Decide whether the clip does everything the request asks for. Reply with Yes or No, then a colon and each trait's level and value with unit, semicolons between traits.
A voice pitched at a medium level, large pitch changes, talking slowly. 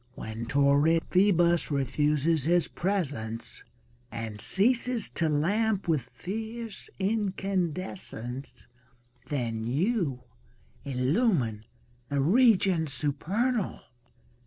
Yes: medium, 165 Hz; wide, 6.7 semitones; slow, 80 wpm